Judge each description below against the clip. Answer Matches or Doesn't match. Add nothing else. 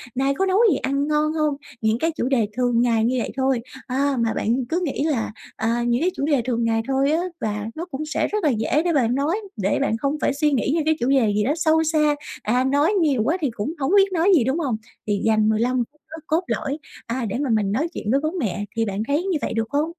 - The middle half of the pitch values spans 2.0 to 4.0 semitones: Doesn't match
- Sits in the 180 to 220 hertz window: Doesn't match